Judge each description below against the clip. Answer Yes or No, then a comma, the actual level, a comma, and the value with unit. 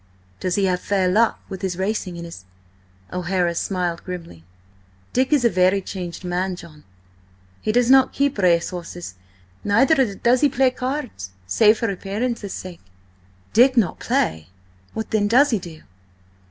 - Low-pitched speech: No, high, 195 Hz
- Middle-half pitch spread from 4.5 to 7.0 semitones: Yes, average, 5.1 semitones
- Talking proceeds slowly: No, average, 155 wpm